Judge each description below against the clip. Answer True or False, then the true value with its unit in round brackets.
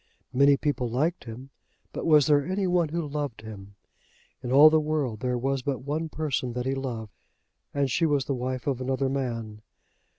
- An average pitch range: True (3.2 semitones)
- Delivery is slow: False (190 wpm)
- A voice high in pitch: False (135 Hz)